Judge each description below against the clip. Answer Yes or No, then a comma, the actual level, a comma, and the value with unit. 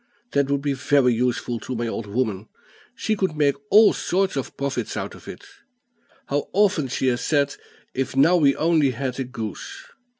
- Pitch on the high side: No, medium, 140 Hz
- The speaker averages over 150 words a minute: Yes, average, 185 wpm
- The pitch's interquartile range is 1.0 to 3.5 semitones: No, average, 4.0 semitones